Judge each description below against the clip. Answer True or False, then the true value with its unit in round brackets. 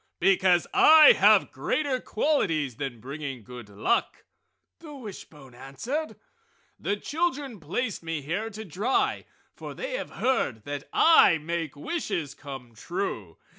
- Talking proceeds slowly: True (130 wpm)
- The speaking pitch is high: False (170 Hz)